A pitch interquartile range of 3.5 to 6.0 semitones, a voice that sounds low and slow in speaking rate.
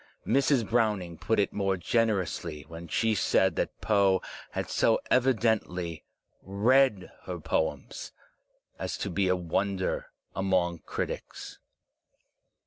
Yes: average, 4.0 semitones; very low, 95 Hz; slow, 115 wpm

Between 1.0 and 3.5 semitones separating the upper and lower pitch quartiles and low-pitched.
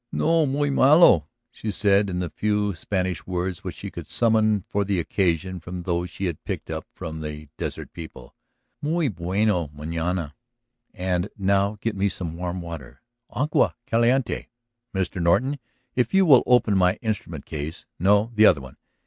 No: average, 4.2 semitones; very low, 95 Hz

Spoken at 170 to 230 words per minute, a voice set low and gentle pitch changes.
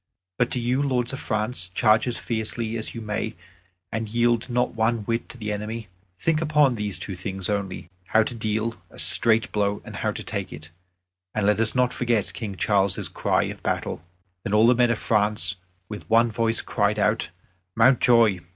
Yes: average, 190 wpm; low, 110 Hz; narrow, 2.3 semitones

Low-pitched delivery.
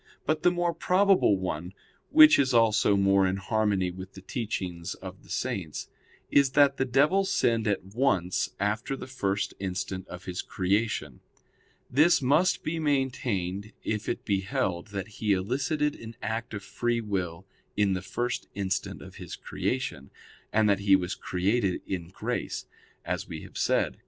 Yes: low, 105 Hz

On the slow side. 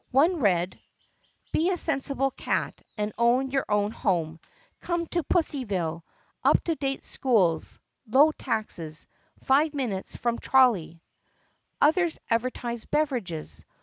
Yes: slow, 115 wpm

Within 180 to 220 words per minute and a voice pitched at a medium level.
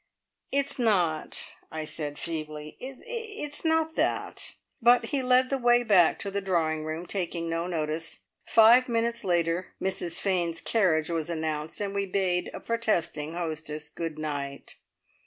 No: average, 145 wpm; medium, 175 Hz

